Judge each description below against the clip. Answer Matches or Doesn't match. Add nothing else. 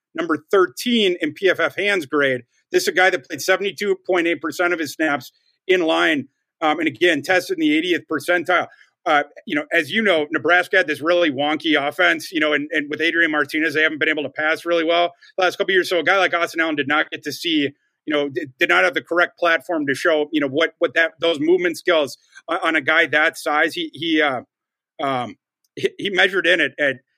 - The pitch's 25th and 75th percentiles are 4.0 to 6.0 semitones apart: Doesn't match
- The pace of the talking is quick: Matches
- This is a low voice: Doesn't match